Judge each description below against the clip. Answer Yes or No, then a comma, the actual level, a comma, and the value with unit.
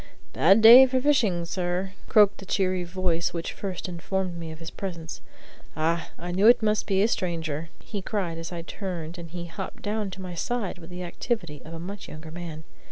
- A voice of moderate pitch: Yes, medium, 180 Hz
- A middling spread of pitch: Yes, average, 3.1 semitones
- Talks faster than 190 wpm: Yes, fast, 205 wpm